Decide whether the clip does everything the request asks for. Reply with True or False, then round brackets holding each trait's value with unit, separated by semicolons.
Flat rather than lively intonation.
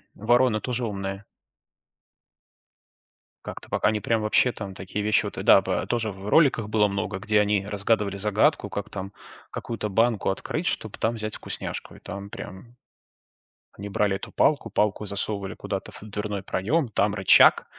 True (1.9 semitones)